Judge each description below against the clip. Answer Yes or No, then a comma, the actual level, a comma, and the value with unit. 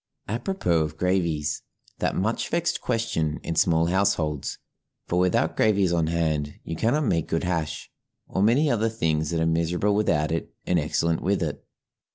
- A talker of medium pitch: No, very low, 85 Hz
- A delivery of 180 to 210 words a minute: No, average, 160 wpm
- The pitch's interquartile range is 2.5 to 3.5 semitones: No, average, 4.4 semitones